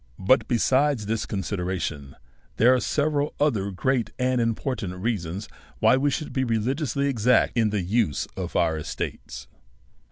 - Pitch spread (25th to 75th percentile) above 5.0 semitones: Yes, wide, 5.6 semitones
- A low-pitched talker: Yes, low, 115 Hz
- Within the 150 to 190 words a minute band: No, average, 140 wpm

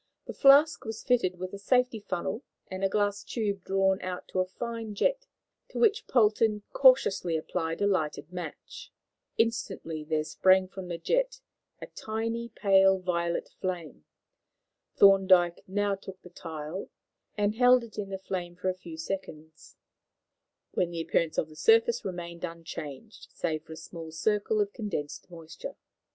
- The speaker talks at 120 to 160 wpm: Yes, average, 155 wpm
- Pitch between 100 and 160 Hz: No, high, 190 Hz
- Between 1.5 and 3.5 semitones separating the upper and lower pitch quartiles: No, average, 4.2 semitones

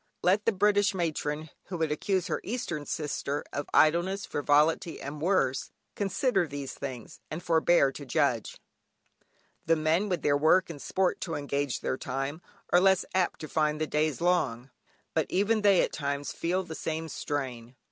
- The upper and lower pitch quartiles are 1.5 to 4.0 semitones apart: No, average, 4.4 semitones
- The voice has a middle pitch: Yes, medium, 160 Hz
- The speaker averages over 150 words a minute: Yes, average, 165 wpm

